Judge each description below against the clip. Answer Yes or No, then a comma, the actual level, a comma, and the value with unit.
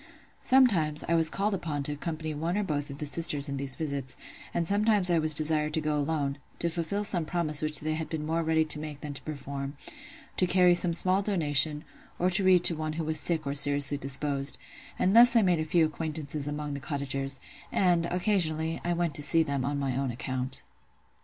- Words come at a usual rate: No, fast, 210 wpm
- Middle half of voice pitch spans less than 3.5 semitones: Yes, average, 3.1 semitones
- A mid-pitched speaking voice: Yes, medium, 155 Hz